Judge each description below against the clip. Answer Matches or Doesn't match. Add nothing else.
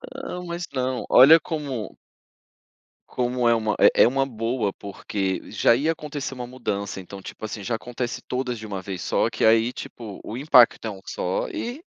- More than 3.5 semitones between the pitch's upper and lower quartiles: Matches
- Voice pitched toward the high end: Doesn't match